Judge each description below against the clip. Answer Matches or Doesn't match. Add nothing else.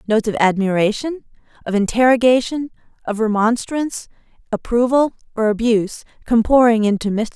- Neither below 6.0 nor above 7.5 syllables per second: Matches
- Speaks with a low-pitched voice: Doesn't match